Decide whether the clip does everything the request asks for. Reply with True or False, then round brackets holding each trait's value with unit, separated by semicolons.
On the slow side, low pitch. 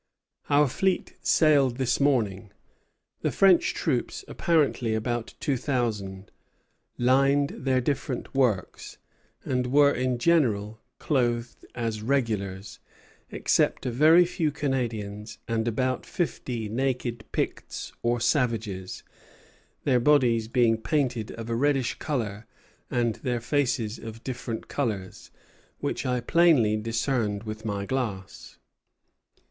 True (115 wpm; 120 Hz)